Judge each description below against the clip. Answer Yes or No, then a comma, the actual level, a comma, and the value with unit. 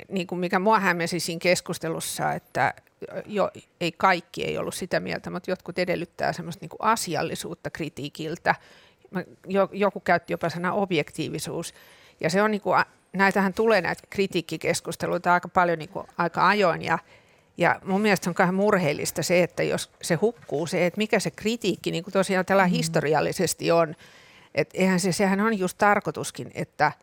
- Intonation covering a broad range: No, narrow, 2.6 semitones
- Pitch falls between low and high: Yes, medium, 180 Hz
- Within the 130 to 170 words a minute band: Yes, fast, 155 wpm